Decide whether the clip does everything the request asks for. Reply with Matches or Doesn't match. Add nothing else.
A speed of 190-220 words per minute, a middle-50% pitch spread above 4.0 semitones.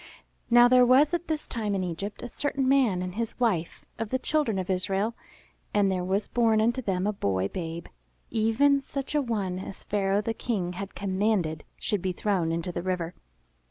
Matches